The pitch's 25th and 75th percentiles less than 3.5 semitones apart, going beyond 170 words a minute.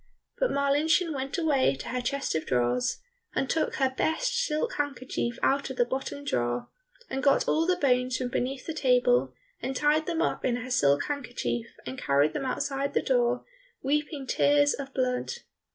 Yes: average, 3.1 semitones; average, 180 wpm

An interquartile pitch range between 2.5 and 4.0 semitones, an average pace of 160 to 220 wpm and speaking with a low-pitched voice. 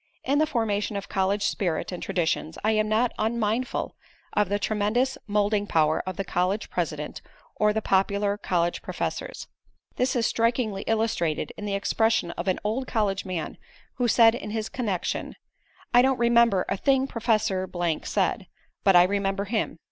No: average, 3.2 semitones; average, 165 wpm; high, 210 Hz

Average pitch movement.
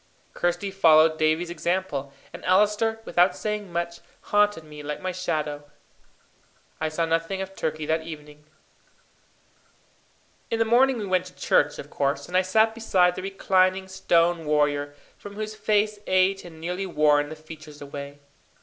Yes: average, 4.0 semitones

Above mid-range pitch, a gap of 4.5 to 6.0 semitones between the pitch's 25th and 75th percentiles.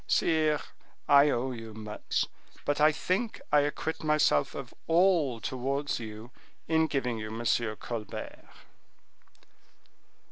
No: medium, 140 Hz; average, 5.3 semitones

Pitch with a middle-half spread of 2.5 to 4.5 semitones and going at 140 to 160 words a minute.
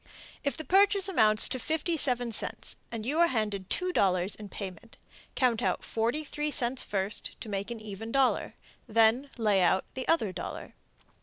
No: wide, 5.5 semitones; average, 155 wpm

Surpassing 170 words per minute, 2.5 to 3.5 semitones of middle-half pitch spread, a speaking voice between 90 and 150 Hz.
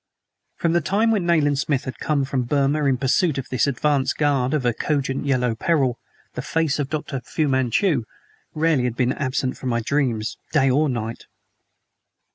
Yes: average, 180 wpm; average, 3.2 semitones; medium, 140 Hz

